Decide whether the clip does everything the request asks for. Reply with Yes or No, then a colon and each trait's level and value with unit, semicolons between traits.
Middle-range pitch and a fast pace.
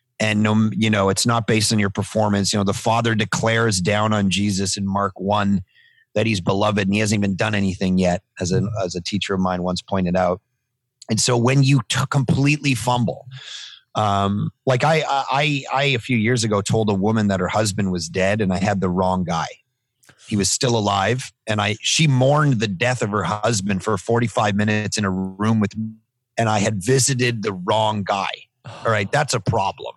No: low, 110 Hz; fast, 210 wpm